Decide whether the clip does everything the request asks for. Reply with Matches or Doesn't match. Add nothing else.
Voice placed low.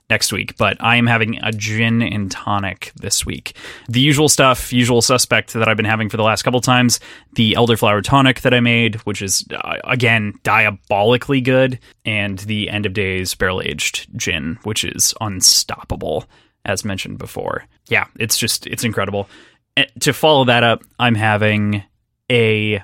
Matches